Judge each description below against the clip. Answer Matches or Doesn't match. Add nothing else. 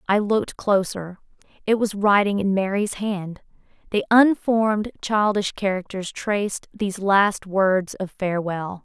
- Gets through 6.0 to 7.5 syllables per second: Doesn't match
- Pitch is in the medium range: Doesn't match